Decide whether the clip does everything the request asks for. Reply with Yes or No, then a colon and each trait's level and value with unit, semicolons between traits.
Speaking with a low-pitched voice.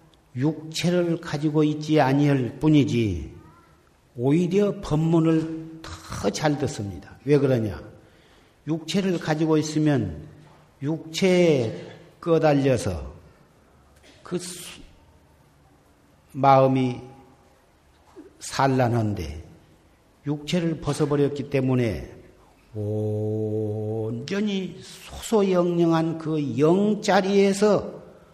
No: medium, 145 Hz